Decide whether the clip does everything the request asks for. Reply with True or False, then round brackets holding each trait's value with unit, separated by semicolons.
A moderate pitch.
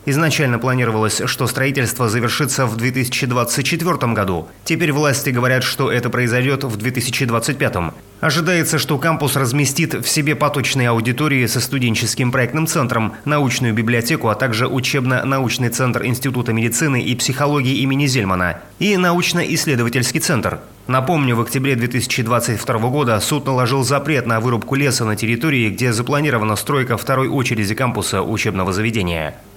False (130 Hz)